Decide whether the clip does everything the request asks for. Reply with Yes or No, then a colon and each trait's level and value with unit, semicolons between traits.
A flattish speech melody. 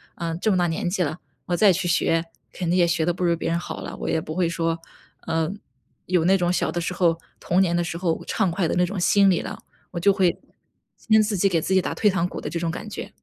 Yes: narrow, 2.0 semitones